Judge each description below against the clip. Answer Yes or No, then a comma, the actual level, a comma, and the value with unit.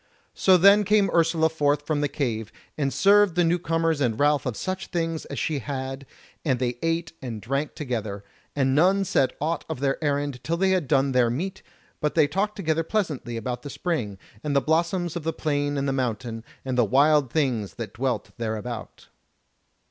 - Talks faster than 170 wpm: Yes, average, 195 wpm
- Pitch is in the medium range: Yes, medium, 145 Hz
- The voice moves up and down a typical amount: Yes, average, 4.5 semitones